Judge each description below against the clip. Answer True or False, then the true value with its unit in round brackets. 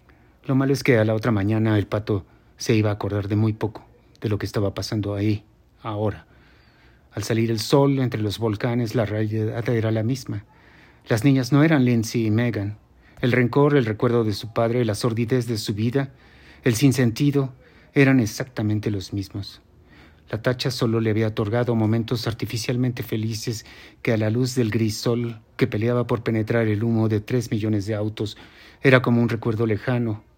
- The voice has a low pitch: True (115 Hz)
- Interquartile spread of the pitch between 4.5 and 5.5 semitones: False (2.7 semitones)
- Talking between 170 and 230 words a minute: True (185 wpm)